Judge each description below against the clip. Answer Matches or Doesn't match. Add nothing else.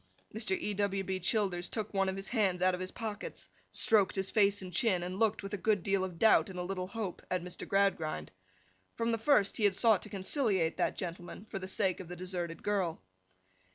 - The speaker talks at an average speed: Doesn't match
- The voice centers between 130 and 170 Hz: Doesn't match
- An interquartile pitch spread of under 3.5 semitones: Matches